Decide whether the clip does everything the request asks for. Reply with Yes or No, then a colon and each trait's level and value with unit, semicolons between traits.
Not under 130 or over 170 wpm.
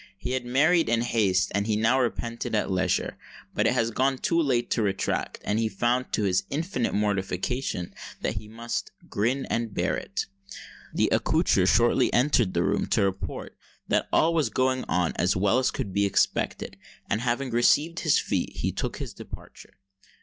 No: average, 180 wpm